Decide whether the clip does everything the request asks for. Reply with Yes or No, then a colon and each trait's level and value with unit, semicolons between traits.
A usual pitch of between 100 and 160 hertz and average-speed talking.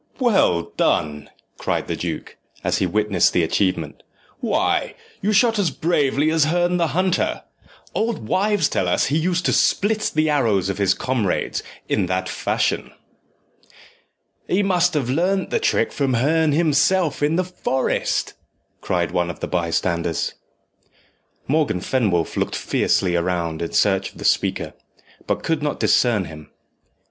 Yes: medium, 140 Hz; average, 150 wpm